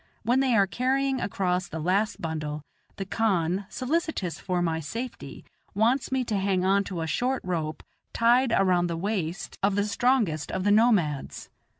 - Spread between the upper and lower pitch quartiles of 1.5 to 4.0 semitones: No, wide, 5.5 semitones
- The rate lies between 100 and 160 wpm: No, average, 170 wpm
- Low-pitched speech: No, high, 195 Hz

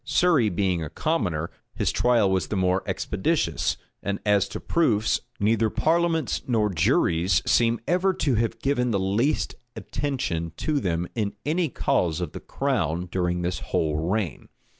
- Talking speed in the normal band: Yes, average, 155 wpm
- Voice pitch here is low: Yes, low, 105 Hz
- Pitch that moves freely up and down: Yes, wide, 7.4 semitones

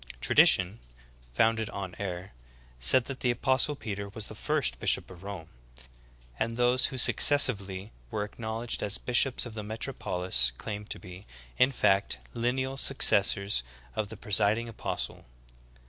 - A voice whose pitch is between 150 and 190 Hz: No, low, 110 Hz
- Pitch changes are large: No, average, 3.8 semitones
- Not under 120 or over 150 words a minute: Yes, average, 145 wpm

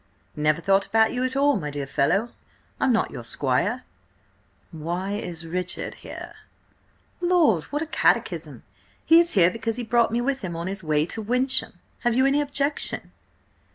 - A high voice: Yes, high, 225 Hz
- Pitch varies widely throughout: Yes, wide, 7.6 semitones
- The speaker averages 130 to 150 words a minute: No, average, 170 wpm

